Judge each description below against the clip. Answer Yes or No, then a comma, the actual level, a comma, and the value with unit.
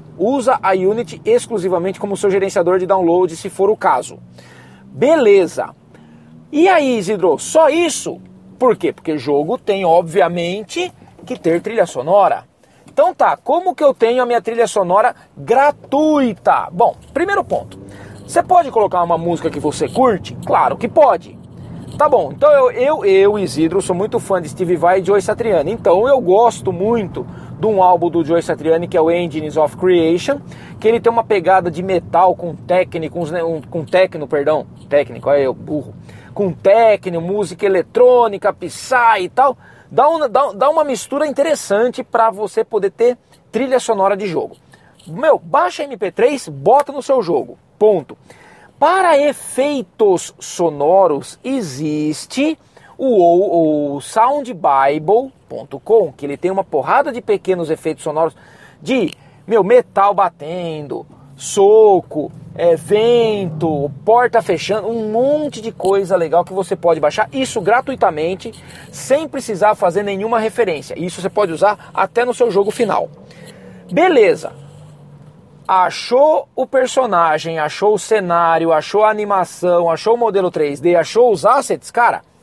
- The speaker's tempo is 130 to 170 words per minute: Yes, average, 145 wpm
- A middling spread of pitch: No, wide, 6.7 semitones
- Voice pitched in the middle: No, high, 200 Hz